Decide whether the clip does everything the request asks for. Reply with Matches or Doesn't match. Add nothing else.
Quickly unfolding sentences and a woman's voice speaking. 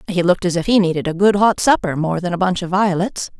Matches